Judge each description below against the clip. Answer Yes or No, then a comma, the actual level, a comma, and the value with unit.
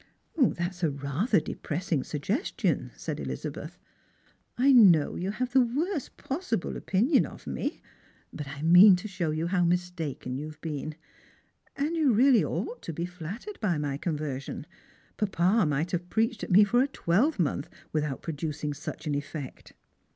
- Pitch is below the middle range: No, medium, 175 Hz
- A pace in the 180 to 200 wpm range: No, average, 160 wpm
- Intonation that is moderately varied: No, wide, 7.0 semitones